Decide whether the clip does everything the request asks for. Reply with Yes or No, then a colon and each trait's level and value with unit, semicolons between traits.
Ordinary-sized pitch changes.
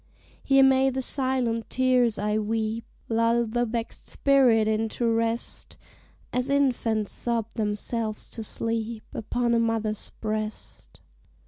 No: narrow, 2.0 semitones